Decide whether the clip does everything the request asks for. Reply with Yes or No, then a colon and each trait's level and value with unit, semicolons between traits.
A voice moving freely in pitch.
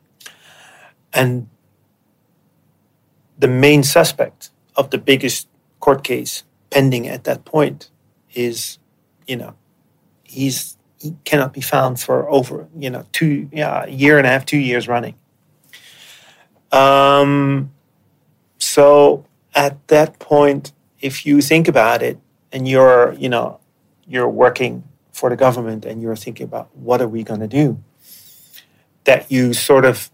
No: average, 2.7 semitones